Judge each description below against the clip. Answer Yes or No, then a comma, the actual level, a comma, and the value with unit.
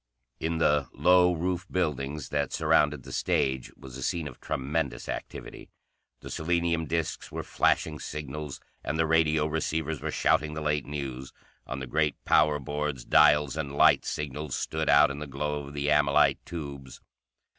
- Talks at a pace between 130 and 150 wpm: No, average, 165 wpm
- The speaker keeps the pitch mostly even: Yes, narrow, 2.1 semitones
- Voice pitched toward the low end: Yes, very low, 75 Hz